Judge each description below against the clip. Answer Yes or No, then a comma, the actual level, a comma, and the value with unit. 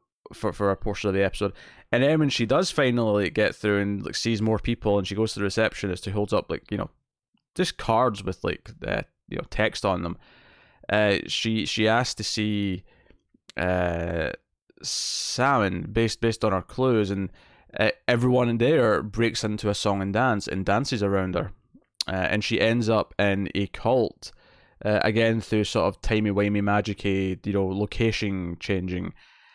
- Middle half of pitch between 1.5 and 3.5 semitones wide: Yes, narrow, 2.4 semitones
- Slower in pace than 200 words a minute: Yes, average, 185 wpm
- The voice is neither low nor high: No, low, 105 Hz